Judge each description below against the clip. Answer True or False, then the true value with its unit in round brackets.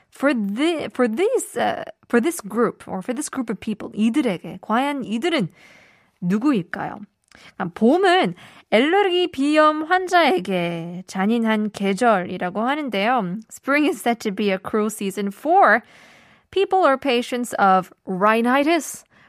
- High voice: True (235 Hz)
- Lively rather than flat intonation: True (6.6 semitones)